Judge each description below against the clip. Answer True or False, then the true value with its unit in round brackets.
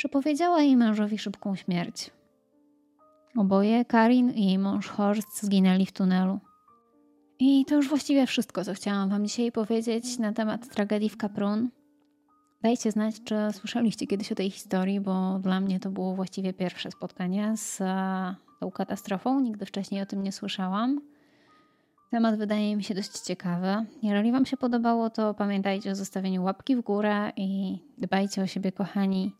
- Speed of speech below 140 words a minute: False (155 wpm)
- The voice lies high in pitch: True (210 Hz)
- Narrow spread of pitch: False (3.7 semitones)